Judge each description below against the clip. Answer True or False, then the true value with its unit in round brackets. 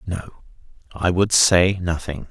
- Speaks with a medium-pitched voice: False (90 Hz)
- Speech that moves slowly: True (130 wpm)